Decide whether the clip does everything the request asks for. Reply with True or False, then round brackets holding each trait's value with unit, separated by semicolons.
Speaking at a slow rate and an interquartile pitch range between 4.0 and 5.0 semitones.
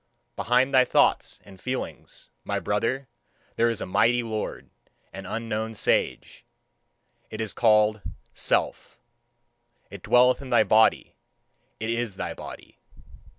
False (125 wpm; 2.4 semitones)